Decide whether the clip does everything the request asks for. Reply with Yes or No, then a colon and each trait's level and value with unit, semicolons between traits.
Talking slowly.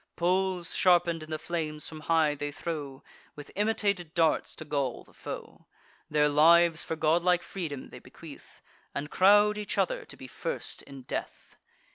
No: average, 160 wpm